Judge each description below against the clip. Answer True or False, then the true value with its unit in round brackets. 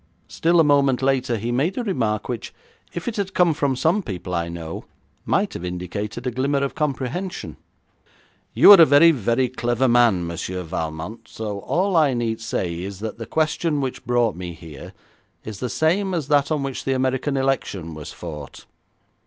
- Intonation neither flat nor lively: False (6.7 semitones)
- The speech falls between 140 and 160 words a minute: False (185 wpm)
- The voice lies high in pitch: False (125 Hz)